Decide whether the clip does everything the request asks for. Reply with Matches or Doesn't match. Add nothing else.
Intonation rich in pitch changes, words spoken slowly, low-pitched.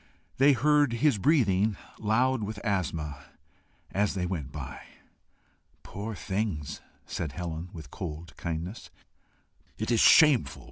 Matches